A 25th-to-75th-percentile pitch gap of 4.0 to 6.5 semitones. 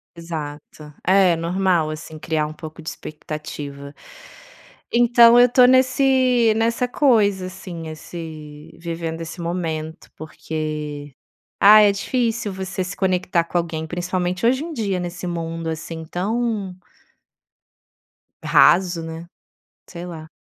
Yes: average, 4.3 semitones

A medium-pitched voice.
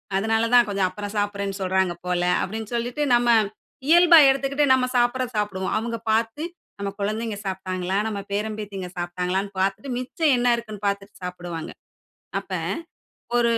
No: high, 210 Hz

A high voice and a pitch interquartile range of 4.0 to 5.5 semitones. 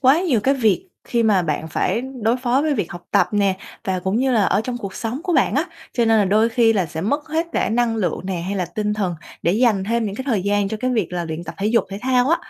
Yes: high, 220 Hz; average, 4.4 semitones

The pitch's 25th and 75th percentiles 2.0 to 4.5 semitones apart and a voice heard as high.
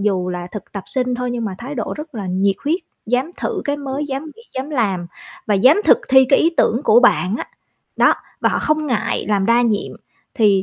No: average, 5.3 semitones; high, 240 Hz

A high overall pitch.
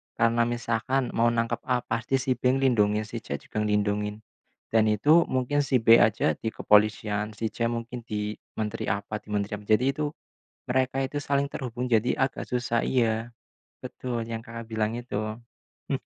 No: low, 115 Hz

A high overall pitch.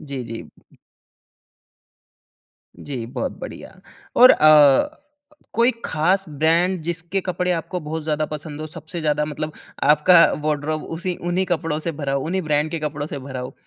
No: medium, 155 Hz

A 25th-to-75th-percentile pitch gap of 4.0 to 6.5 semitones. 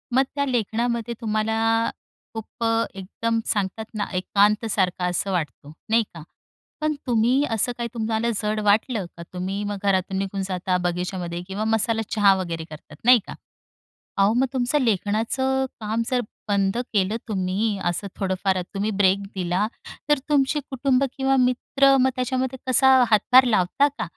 Yes: average, 4.3 semitones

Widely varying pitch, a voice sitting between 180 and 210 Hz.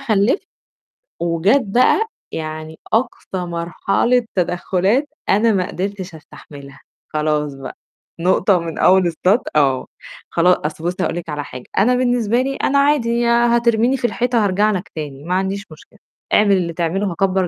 Yes: wide, 5.9 semitones; high, 190 Hz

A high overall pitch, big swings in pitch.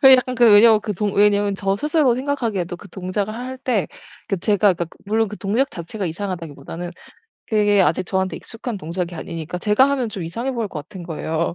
No: high, 205 Hz; average, 4.4 semitones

